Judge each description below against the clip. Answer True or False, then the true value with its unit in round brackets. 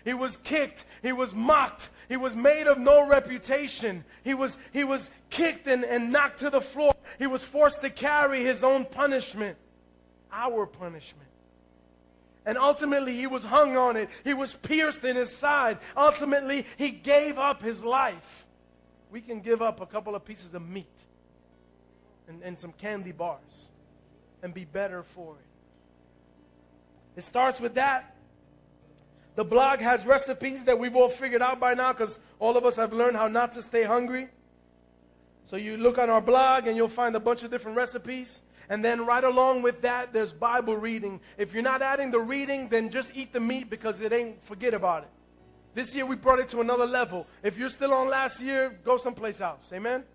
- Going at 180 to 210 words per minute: True (185 wpm)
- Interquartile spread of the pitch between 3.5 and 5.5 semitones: True (5.0 semitones)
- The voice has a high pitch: True (245 Hz)